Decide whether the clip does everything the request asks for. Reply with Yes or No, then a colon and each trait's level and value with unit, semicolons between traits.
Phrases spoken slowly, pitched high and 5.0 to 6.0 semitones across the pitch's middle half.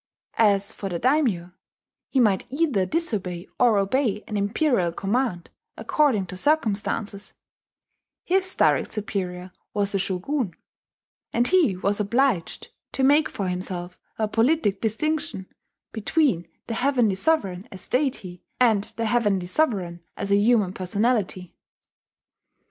Yes: slow, 125 wpm; high, 210 Hz; wide, 5.4 semitones